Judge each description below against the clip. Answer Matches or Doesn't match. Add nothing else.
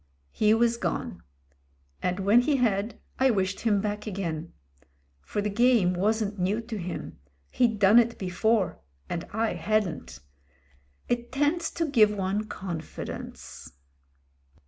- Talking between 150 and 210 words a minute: Doesn't match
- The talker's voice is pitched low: Doesn't match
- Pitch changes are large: Doesn't match